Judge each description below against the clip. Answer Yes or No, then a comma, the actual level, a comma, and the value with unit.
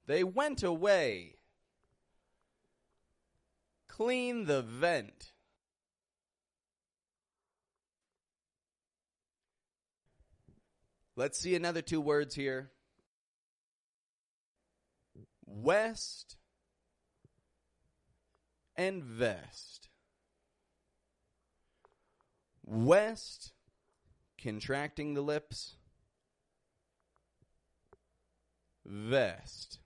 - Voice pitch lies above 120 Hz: Yes, medium, 140 Hz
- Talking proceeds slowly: Yes, slow, 40 wpm